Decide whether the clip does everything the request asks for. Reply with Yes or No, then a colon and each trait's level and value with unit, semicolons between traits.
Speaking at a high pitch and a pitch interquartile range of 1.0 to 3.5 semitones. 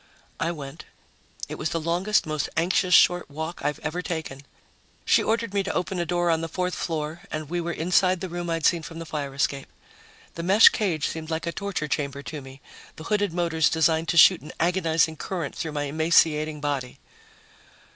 No: medium, 165 Hz; narrow, 2.4 semitones